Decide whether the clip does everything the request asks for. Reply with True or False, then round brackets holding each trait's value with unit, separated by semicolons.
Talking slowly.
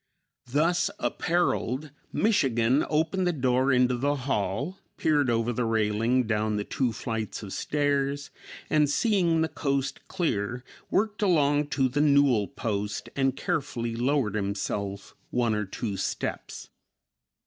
True (130 wpm)